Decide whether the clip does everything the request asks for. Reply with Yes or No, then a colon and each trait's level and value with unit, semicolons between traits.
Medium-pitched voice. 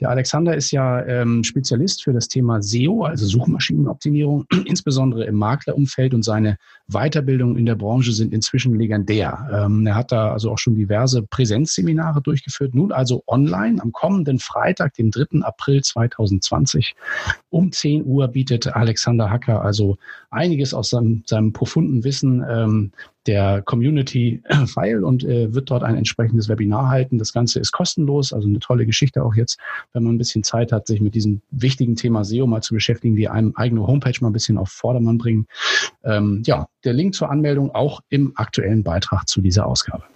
No: low, 120 Hz